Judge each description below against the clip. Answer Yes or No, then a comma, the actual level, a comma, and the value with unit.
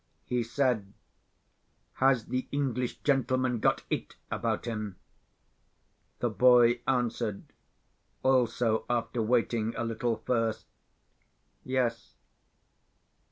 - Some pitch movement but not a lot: No, narrow, 2.0 semitones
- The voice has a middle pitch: No, low, 120 Hz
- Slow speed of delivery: Yes, slow, 80 wpm